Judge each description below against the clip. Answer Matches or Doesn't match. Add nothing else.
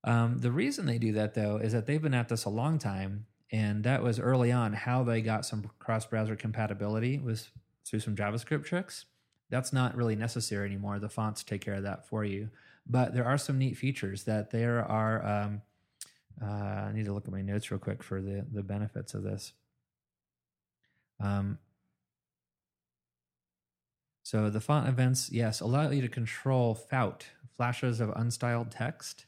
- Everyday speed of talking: Matches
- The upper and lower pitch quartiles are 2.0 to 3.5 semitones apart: Matches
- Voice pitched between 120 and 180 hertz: Doesn't match